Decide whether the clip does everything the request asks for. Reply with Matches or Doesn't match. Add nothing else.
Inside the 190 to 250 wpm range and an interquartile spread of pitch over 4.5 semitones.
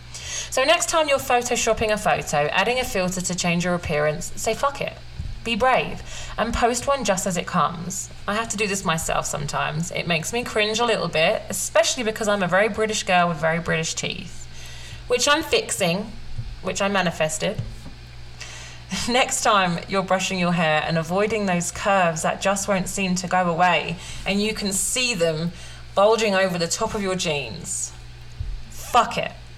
Doesn't match